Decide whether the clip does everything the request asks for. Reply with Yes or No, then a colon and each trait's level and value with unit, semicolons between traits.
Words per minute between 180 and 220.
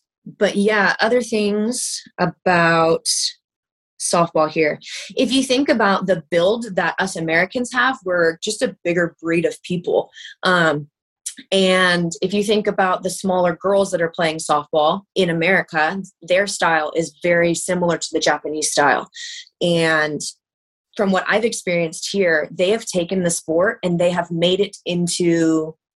No: average, 150 wpm